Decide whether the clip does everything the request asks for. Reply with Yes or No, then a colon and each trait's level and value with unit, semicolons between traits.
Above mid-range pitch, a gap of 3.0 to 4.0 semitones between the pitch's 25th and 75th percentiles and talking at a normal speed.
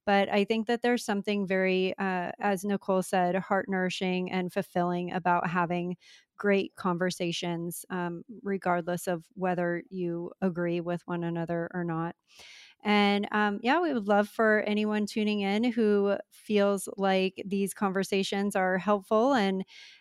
No: high, 195 Hz; narrow, 2.4 semitones; average, 145 wpm